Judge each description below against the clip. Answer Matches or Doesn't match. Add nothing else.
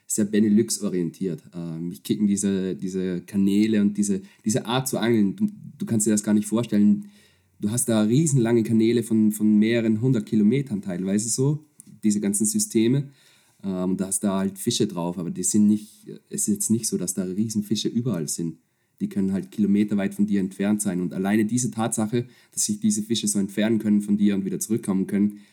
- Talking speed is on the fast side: Matches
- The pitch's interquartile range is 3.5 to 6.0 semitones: Doesn't match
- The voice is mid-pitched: Doesn't match